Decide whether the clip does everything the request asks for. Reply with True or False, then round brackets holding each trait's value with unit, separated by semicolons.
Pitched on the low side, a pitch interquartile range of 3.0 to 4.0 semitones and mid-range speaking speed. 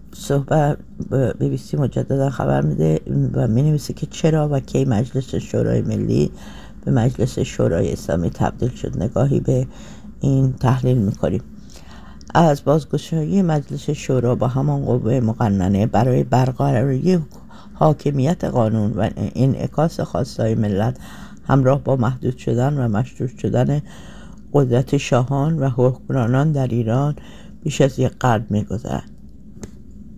False (130 Hz; 3.3 semitones; 130 wpm)